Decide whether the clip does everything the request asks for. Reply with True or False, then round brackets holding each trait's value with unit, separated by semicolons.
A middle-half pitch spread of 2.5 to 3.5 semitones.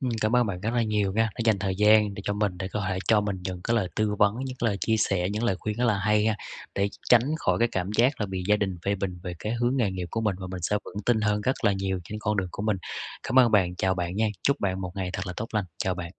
True (2.8 semitones)